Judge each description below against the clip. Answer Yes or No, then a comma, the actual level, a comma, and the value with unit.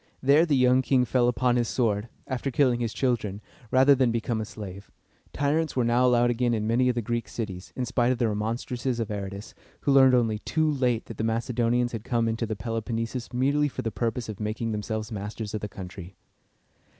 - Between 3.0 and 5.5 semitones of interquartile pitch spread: No, narrow, 2.6 semitones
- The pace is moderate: No, fast, 210 wpm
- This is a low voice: Yes, low, 120 Hz